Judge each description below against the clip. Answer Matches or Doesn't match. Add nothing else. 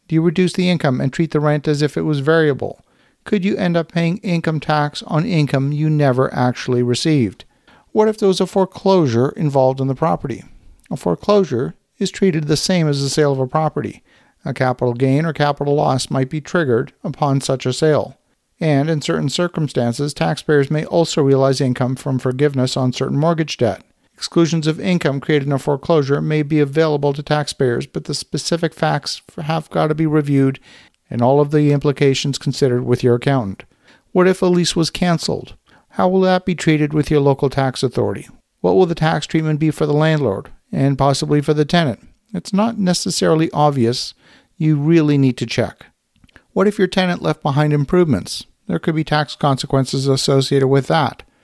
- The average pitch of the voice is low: Doesn't match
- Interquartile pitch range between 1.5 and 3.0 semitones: Doesn't match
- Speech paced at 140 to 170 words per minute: Doesn't match